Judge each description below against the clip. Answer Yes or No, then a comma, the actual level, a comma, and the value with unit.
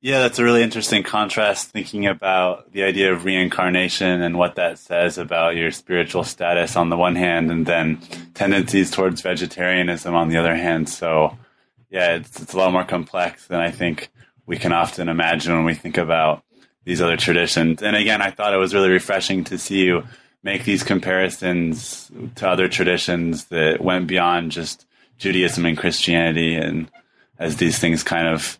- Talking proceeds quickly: No, average, 180 wpm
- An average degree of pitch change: No, narrow, 2.0 semitones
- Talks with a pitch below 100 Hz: Yes, very low, 90 Hz